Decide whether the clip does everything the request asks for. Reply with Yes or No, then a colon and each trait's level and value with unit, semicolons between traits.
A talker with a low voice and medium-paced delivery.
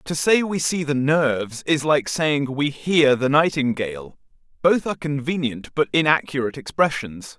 No: medium, 145 Hz; average, 155 wpm